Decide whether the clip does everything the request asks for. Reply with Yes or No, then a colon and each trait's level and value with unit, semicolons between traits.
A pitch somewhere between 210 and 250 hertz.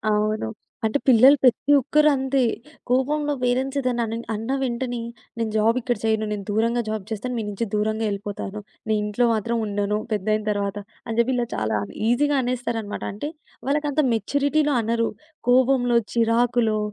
Yes: high, 235 Hz